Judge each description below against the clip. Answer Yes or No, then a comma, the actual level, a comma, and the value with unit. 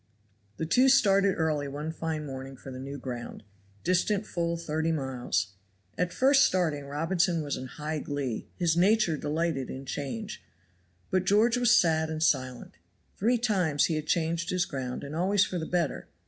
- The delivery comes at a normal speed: Yes, average, 170 wpm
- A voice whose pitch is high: No, medium, 160 Hz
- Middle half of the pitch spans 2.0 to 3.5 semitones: No, average, 4.6 semitones